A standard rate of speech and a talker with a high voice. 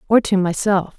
Yes: average, 180 wpm; high, 195 Hz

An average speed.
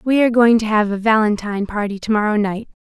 No: fast, 235 wpm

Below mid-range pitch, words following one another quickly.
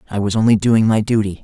Yes: low, 105 Hz; fast, 250 wpm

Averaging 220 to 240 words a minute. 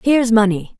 Yes: fast, 230 wpm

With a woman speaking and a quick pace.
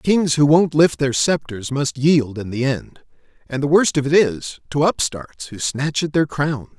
No: male; fast, 210 wpm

